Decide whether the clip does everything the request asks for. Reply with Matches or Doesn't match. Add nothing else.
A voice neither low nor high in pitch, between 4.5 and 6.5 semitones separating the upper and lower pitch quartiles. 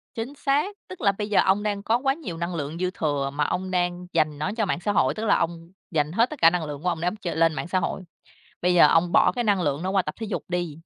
Doesn't match